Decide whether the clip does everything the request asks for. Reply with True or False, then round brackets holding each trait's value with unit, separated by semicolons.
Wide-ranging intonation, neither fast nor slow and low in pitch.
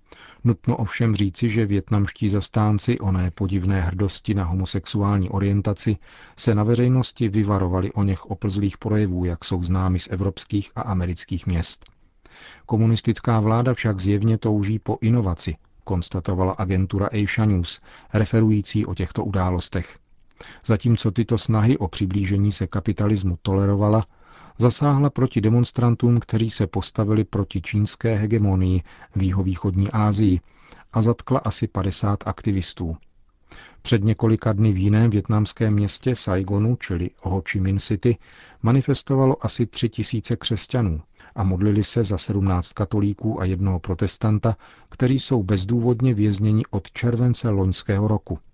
False (2.8 semitones; 125 wpm; 105 Hz)